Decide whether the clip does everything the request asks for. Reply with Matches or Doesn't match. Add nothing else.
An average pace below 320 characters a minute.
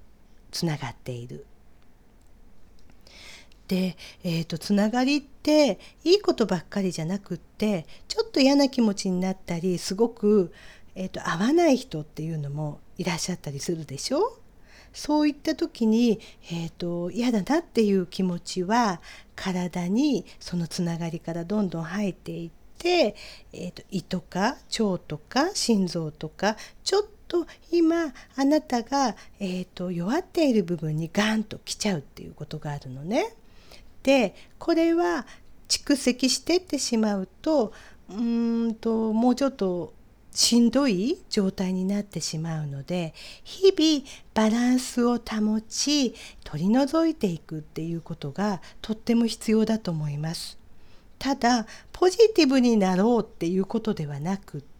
Matches